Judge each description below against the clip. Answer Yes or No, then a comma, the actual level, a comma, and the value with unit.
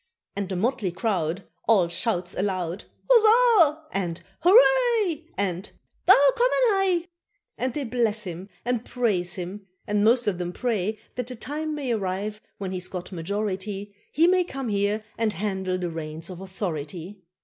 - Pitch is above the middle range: Yes, high, 205 Hz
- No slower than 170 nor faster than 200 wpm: No, average, 160 wpm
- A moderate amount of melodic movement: No, wide, 6.7 semitones